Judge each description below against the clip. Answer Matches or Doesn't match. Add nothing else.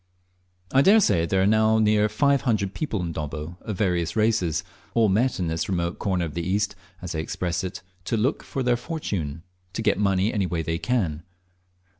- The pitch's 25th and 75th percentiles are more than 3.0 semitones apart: Matches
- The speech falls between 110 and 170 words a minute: Doesn't match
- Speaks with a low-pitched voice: Matches